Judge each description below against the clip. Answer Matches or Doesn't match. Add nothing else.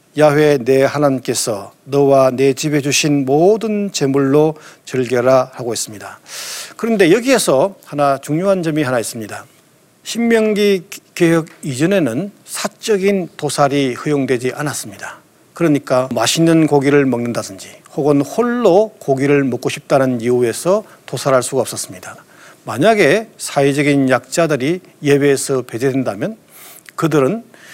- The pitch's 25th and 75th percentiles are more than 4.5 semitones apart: Doesn't match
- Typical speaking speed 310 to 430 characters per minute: Doesn't match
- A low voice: Doesn't match